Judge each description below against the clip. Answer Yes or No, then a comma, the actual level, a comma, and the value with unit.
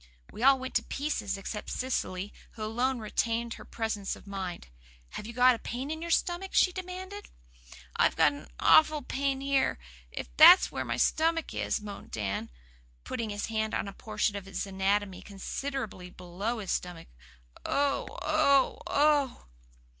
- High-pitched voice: Yes, high, 230 Hz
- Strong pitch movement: Yes, wide, 5.9 semitones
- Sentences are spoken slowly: No, average, 160 wpm